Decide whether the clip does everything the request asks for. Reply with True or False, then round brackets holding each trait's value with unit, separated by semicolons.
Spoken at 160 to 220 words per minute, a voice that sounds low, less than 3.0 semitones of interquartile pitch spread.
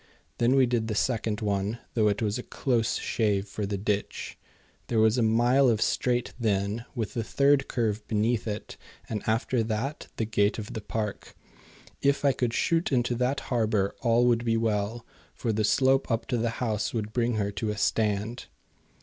True (190 wpm; 115 Hz; 2.4 semitones)